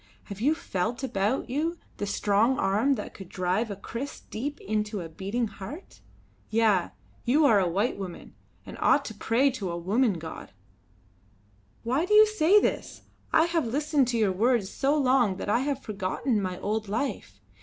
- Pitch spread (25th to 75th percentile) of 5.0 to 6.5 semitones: Yes, wide, 5.5 semitones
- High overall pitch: Yes, high, 225 Hz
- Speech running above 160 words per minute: Yes, average, 175 wpm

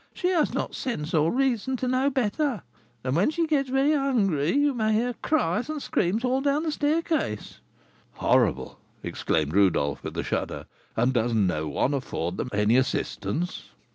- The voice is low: No, high, 220 Hz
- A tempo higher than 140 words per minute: Yes, average, 170 wpm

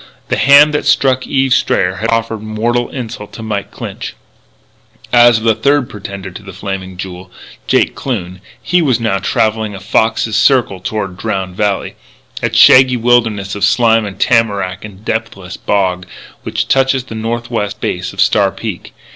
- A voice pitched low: Yes, low, 110 Hz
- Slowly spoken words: No, average, 165 wpm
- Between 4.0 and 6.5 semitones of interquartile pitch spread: No, average, 3.6 semitones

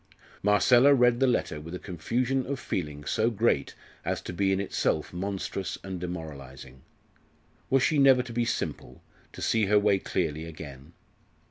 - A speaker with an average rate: Yes, average, 160 wpm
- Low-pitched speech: Yes, very low, 95 Hz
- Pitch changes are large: Yes, wide, 7.2 semitones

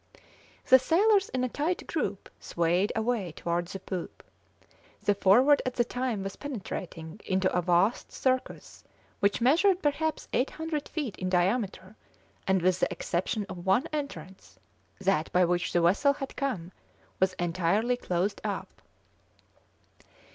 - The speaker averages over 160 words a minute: No, average, 140 wpm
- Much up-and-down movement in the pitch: Yes, wide, 6.4 semitones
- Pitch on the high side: Yes, high, 200 Hz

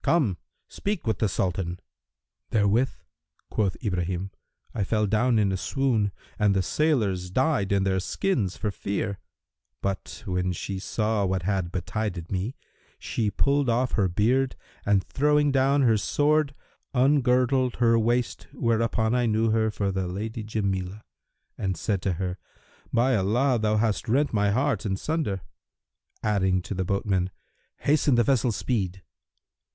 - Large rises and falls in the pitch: No, average, 4.6 semitones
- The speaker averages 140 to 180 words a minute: Yes, average, 145 wpm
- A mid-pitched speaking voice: No, low, 105 Hz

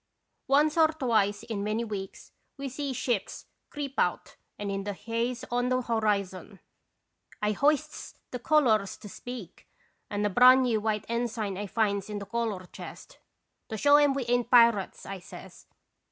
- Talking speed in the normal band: Yes, average, 170 wpm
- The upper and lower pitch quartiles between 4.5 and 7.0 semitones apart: No, average, 3.7 semitones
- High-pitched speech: Yes, high, 230 Hz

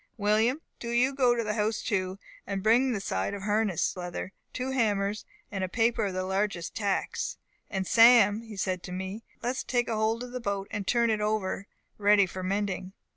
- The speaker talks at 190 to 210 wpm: Yes, average, 200 wpm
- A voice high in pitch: Yes, high, 210 Hz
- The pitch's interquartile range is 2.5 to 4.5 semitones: Yes, average, 3.2 semitones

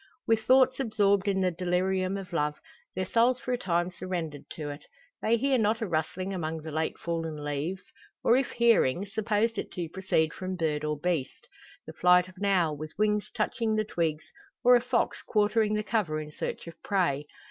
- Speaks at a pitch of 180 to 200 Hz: Yes, medium, 185 Hz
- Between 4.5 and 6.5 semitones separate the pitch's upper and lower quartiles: Yes, average, 5.0 semitones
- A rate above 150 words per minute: Yes, average, 195 wpm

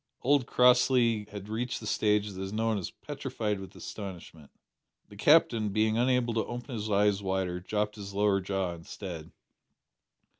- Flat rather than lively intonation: No, average, 3.3 semitones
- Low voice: Yes, low, 105 Hz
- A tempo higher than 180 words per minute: No, average, 155 wpm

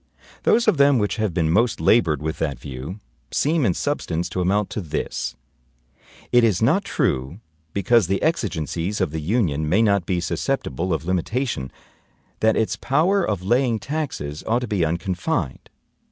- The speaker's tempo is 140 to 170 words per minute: Yes, average, 165 wpm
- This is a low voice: Yes, low, 100 Hz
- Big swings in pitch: Yes, wide, 6.9 semitones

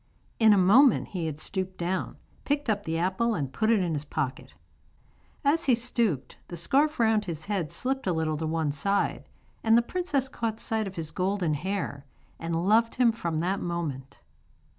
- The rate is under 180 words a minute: No, average, 185 wpm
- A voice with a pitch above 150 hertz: Yes, high, 190 Hz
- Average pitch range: No, wide, 5.9 semitones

